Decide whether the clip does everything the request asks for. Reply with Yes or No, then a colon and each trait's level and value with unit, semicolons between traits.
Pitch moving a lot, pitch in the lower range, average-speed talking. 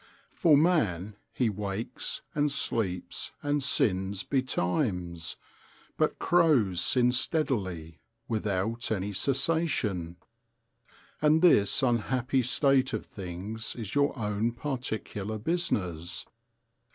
No: wide, 6.2 semitones; low, 110 Hz; slow, 95 wpm